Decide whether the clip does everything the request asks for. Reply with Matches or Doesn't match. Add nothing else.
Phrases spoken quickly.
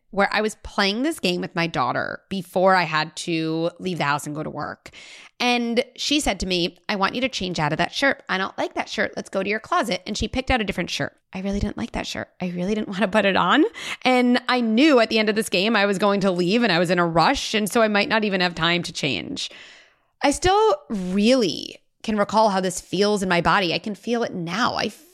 Matches